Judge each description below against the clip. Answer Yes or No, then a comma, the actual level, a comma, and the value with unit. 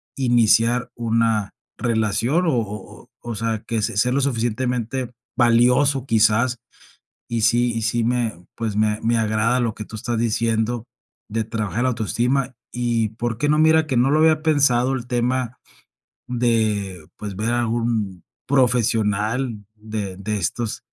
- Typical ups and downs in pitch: No, narrow, 2.3 semitones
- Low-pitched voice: Yes, low, 115 Hz